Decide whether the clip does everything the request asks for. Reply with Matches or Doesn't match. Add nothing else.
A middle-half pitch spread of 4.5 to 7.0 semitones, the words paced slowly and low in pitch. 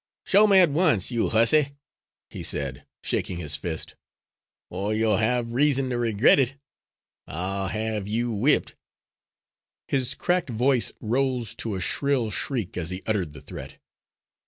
Doesn't match